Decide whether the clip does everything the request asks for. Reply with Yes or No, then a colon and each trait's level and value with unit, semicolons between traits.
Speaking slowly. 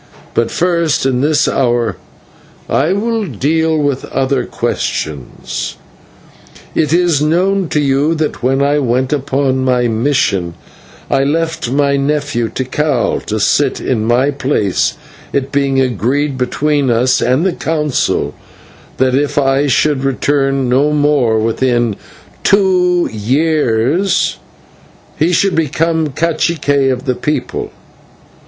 Yes: slow, 120 wpm